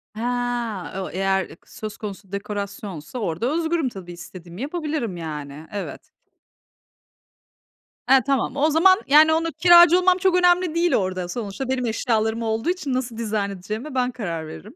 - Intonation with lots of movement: Yes, wide, 8.1 semitones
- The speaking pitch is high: Yes, high, 230 Hz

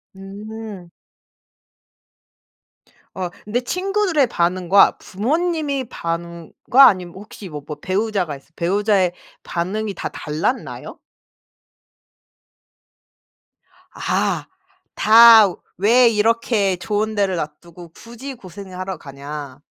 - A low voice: No, high, 200 Hz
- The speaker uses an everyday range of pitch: Yes, average, 4.9 semitones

